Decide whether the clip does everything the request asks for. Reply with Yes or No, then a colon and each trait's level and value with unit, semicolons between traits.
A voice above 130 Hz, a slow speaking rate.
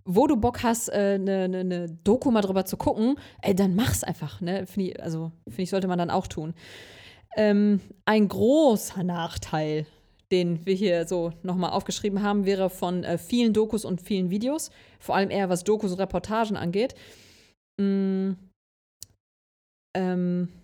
No: high, 190 Hz; average, 165 wpm